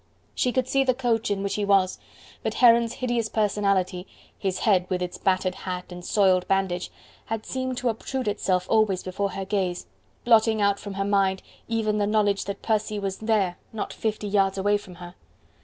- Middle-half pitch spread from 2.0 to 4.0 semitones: Yes, narrow, 2.6 semitones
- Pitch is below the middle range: No, high, 200 Hz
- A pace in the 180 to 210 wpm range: Yes, average, 190 wpm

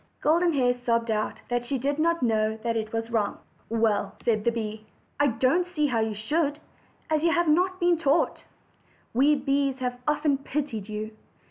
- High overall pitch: Yes, very high, 255 Hz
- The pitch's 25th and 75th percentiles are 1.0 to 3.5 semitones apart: No, average, 5.1 semitones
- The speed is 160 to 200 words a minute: Yes, average, 175 wpm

